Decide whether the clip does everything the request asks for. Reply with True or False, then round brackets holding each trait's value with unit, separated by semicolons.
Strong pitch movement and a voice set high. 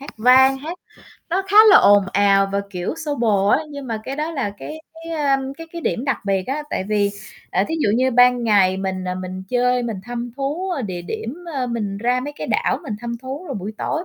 True (5.7 semitones; 245 Hz)